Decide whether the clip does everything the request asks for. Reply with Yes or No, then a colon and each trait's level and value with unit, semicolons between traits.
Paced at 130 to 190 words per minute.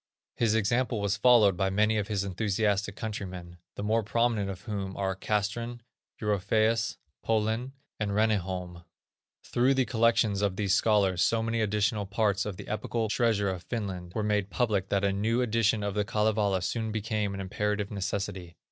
Yes: average, 165 wpm